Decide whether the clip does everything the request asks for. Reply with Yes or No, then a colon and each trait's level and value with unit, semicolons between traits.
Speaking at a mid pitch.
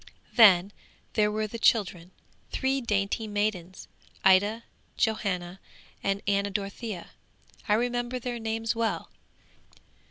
No: high, 210 Hz